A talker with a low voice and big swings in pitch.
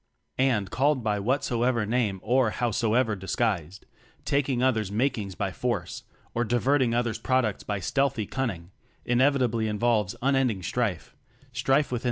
No: low, 120 Hz; average, 3.7 semitones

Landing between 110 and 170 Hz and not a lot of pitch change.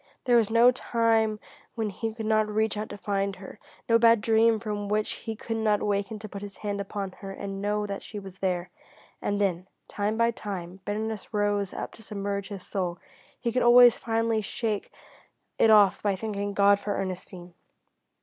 No: high, 210 Hz; narrow, 1.9 semitones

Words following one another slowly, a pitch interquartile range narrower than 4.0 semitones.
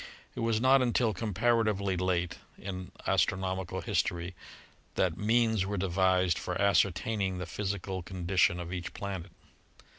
Yes: slow, 130 wpm; narrow, 2.5 semitones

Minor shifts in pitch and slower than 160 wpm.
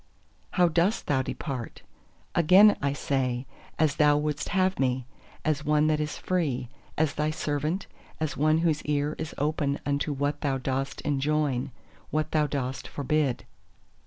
Yes: narrow, 2.0 semitones; average, 150 wpm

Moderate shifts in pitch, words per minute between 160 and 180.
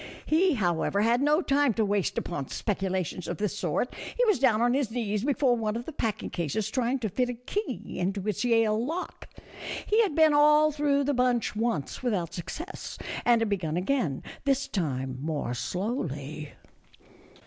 No: wide, 7.1 semitones; average, 175 wpm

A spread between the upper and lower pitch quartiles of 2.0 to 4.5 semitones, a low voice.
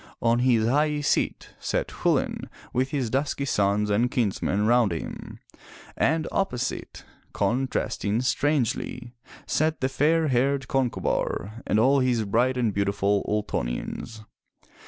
Yes: average, 4.2 semitones; low, 120 Hz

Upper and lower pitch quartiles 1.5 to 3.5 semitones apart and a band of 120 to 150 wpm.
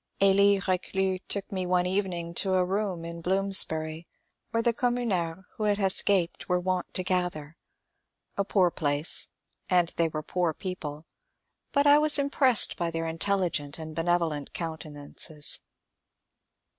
Yes: average, 3.2 semitones; average, 145 wpm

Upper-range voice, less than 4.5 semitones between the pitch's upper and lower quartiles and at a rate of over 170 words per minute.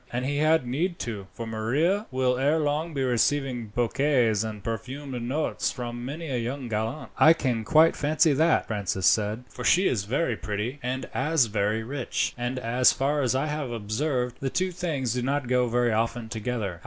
No: low, 125 Hz; average, 4.1 semitones; average, 190 wpm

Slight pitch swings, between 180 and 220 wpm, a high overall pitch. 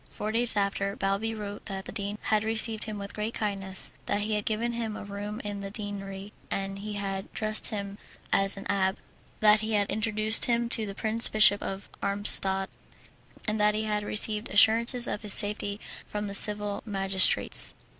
Yes: narrow, 1.5 semitones; average, 185 wpm; high, 210 Hz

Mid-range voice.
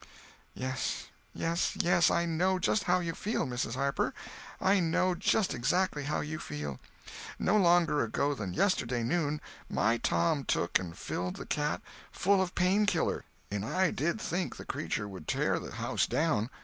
Yes: medium, 155 Hz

